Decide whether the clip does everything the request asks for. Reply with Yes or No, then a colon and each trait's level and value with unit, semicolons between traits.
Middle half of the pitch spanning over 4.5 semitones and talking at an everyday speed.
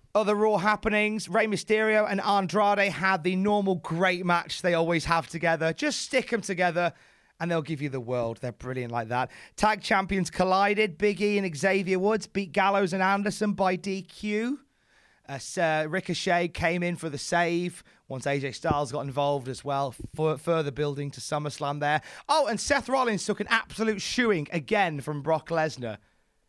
Yes: wide, 5.5 semitones; average, 175 wpm